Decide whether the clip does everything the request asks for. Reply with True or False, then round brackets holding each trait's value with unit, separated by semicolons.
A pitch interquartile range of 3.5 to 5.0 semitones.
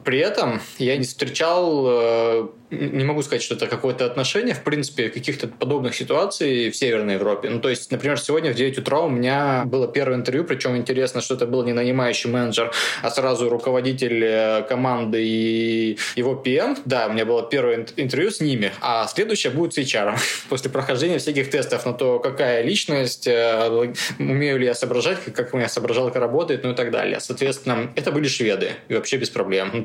False (3.0 semitones)